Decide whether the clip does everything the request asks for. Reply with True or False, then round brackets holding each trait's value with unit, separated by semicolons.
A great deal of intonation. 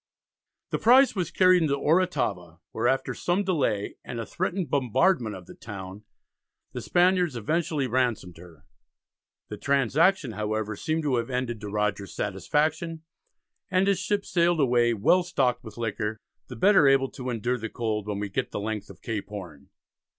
True (7.9 semitones)